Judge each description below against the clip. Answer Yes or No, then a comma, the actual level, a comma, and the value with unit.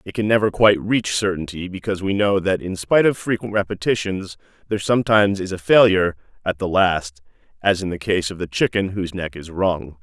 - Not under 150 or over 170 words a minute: No, fast, 205 wpm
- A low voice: Yes, very low, 95 Hz